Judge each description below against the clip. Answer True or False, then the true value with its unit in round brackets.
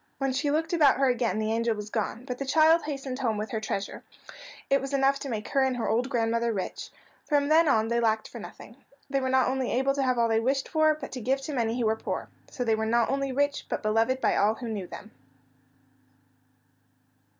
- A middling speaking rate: False (235 wpm)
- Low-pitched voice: False (255 Hz)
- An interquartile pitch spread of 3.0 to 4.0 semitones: True (3.5 semitones)